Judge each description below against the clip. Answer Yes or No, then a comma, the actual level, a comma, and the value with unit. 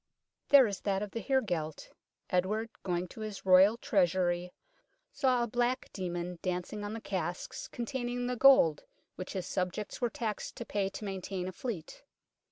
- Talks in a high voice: Yes, high, 200 Hz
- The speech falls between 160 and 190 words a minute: Yes, average, 165 wpm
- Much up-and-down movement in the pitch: No, average, 4.7 semitones